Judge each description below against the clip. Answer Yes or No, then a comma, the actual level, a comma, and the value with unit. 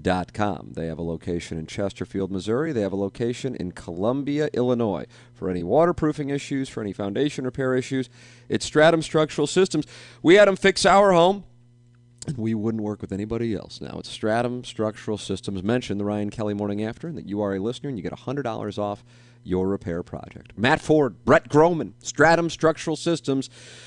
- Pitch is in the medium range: No, low, 120 Hz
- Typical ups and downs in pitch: No, wide, 5.9 semitones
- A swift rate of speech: No, average, 185 wpm